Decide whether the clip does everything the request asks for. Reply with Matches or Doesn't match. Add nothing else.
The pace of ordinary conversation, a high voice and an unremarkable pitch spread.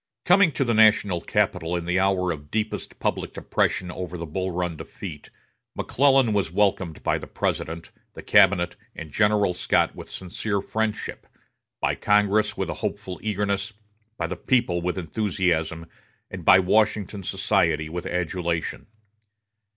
Doesn't match